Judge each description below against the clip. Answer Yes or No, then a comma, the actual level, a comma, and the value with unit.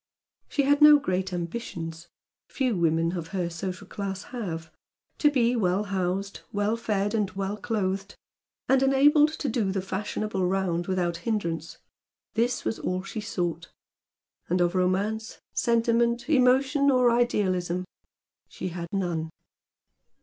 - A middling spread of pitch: Yes, average, 4.7 semitones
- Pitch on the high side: Yes, high, 195 Hz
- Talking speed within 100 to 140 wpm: Yes, slow, 135 wpm